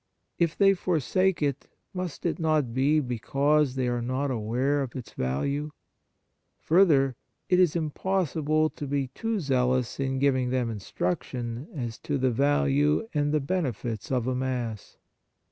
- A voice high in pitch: No, medium, 140 Hz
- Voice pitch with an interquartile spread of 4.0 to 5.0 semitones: No, average, 3.5 semitones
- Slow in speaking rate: No, average, 150 wpm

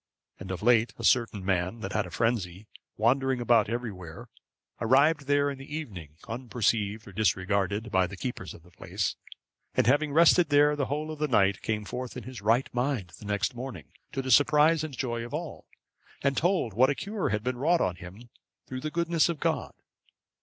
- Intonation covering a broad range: Yes, wide, 5.8 semitones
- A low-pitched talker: Yes, low, 120 Hz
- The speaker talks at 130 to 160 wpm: No, average, 195 wpm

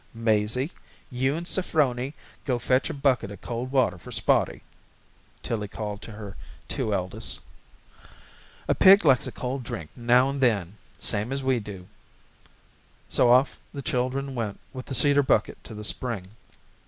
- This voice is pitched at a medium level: No, low, 125 Hz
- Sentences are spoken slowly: No, average, 155 wpm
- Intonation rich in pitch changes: No, average, 4.1 semitones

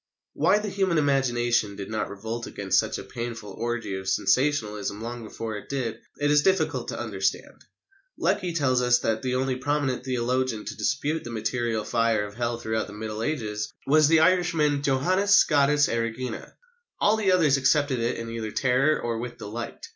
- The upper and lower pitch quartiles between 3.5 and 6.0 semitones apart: Yes, average, 4.6 semitones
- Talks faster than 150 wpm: Yes, average, 180 wpm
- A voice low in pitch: Yes, low, 125 Hz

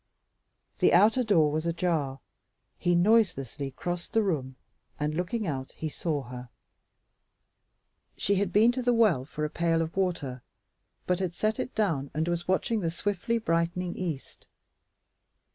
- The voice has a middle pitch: Yes, medium, 175 Hz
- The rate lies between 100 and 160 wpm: Yes, average, 150 wpm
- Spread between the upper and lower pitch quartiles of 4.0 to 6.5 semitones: Yes, average, 4.9 semitones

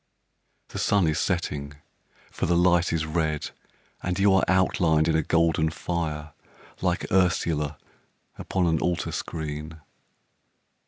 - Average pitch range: No, narrow, 2.2 semitones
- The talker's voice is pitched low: Yes, very low, 80 Hz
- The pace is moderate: No, slow, 125 wpm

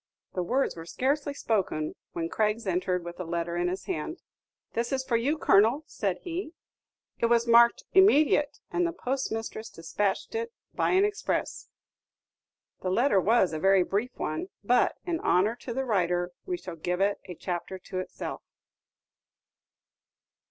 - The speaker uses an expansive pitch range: Yes, wide, 6.8 semitones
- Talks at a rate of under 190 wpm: Yes, average, 160 wpm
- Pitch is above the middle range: Yes, high, 220 Hz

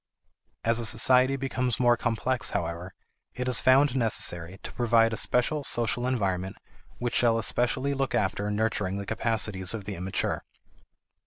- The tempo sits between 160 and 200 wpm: No, average, 150 wpm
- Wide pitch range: No, average, 4.0 semitones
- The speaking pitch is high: No, low, 115 Hz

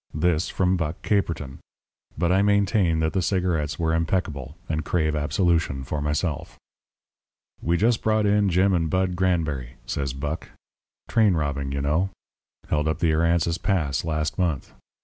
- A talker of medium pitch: No, very low, 85 Hz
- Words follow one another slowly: No, average, 150 wpm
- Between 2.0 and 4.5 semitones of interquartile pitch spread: Yes, average, 3.6 semitones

